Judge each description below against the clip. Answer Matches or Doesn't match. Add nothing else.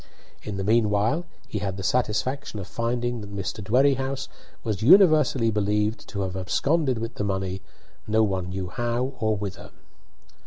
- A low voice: Matches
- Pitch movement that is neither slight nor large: Matches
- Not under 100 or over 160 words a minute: Matches